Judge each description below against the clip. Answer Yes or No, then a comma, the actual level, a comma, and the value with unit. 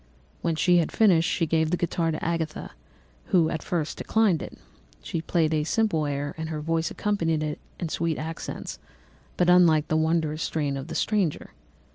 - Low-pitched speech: No, medium, 160 Hz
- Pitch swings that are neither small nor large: No, narrow, 1.8 semitones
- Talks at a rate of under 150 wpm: No, average, 180 wpm